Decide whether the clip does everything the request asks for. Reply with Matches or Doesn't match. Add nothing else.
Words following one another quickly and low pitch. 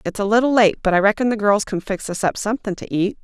Doesn't match